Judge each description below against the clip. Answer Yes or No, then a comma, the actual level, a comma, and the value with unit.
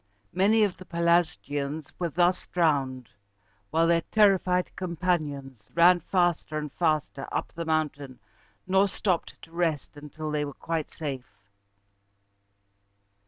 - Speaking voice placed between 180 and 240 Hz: No, medium, 165 Hz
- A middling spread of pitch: Yes, average, 3.4 semitones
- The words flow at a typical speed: No, slow, 120 wpm